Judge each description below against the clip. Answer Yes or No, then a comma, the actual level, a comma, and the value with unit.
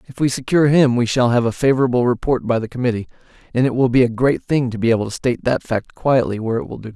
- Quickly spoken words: Yes, fast, 285 wpm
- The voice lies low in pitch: Yes, low, 125 Hz